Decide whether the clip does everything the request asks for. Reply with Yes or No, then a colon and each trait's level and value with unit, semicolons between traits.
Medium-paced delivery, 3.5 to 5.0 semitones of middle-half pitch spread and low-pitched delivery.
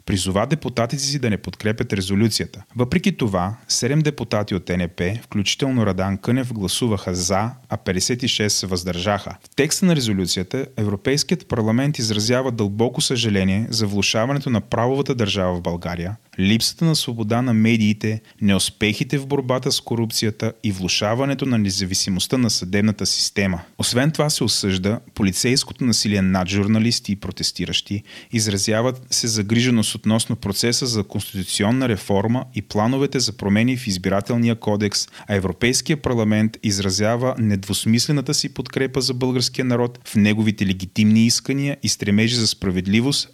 Yes: average, 135 wpm; average, 4.1 semitones; low, 110 Hz